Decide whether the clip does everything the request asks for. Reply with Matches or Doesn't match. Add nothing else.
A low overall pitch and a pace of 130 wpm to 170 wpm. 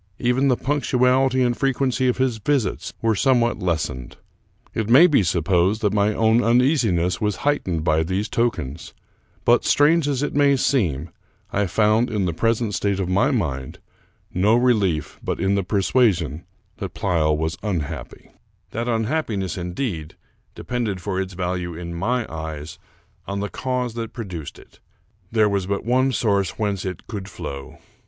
Matches